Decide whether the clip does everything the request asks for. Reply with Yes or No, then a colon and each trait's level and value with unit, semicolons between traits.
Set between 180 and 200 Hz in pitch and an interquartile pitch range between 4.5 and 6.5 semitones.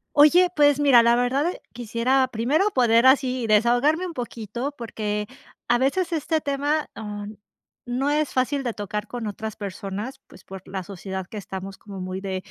No: high, 240 Hz; average, 5.3 semitones